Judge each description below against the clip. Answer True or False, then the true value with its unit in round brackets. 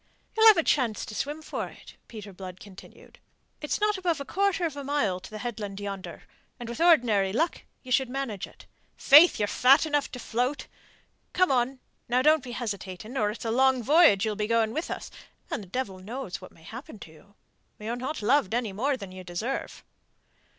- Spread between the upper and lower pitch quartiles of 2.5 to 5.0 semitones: False (5.6 semitones)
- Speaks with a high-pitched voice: True (240 Hz)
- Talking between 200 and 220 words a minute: True (205 wpm)